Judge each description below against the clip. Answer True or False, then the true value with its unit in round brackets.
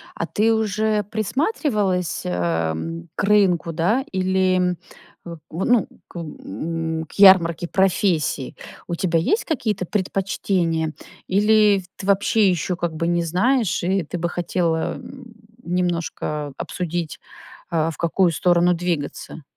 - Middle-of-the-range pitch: True (180 Hz)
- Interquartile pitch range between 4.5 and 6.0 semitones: False (3.4 semitones)